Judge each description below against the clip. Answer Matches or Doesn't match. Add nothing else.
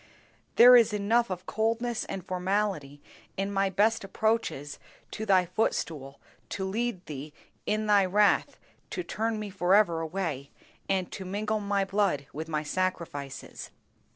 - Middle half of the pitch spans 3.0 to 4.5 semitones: Matches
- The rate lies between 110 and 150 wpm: Matches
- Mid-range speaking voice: Doesn't match